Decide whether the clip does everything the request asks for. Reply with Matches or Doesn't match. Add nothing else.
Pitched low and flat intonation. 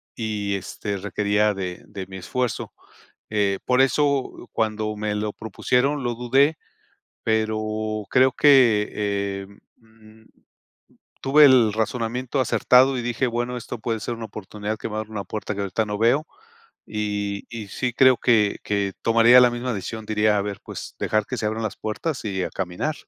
Doesn't match